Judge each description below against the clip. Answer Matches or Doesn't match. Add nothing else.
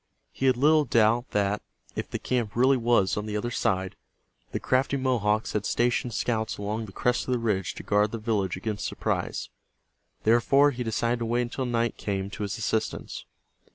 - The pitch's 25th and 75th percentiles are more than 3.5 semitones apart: Doesn't match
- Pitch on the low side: Matches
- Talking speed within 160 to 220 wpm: Matches